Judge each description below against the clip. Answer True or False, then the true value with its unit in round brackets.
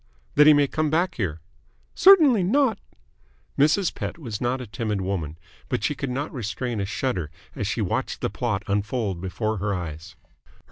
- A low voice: True (120 Hz)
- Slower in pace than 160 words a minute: False (175 wpm)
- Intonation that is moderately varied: False (7.3 semitones)